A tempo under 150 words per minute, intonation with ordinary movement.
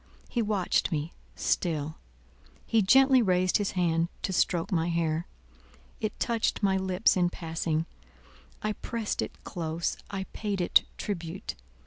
Yes: slow, 135 wpm; average, 3.8 semitones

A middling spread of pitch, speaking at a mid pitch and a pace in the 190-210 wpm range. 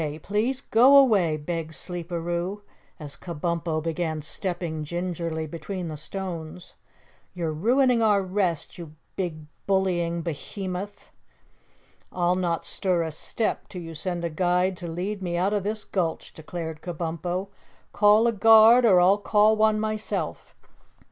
No: average, 3.7 semitones; medium, 180 Hz; slow, 135 wpm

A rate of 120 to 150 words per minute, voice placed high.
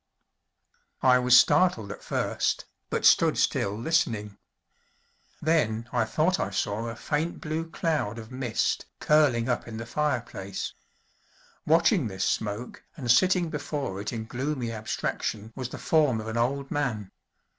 No: average, 145 wpm; low, 125 Hz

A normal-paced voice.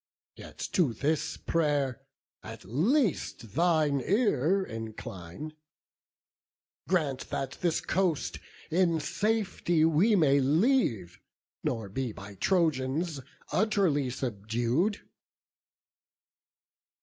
No: slow, 85 wpm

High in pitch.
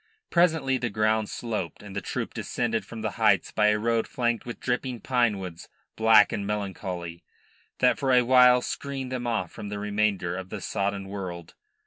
No: low, 110 Hz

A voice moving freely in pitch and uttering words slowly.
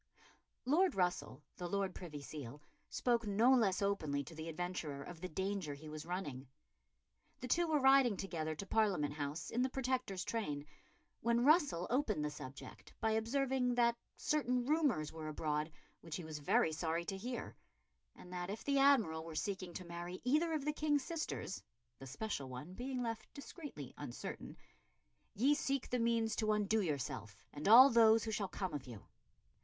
No: wide, 8.1 semitones; average, 175 wpm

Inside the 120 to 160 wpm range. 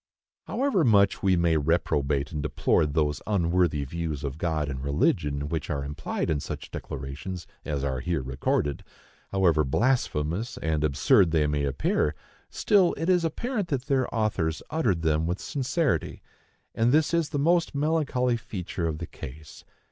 Yes: average, 150 wpm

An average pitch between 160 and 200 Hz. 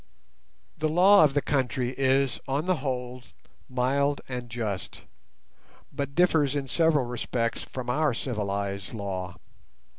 No: low, 130 Hz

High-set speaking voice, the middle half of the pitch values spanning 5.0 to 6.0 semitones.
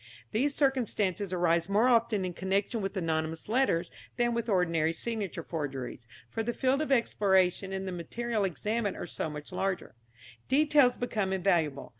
Yes: high, 195 Hz; wide, 5.4 semitones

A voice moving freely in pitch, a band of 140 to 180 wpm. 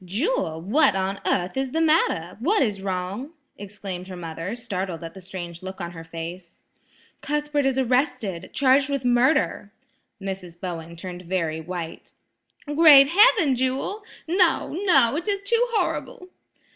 Yes: wide, 8.5 semitones; average, 145 wpm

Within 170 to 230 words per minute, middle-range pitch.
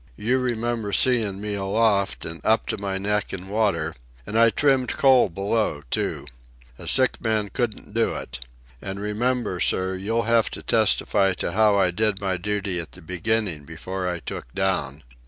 No: average, 175 wpm; low, 100 Hz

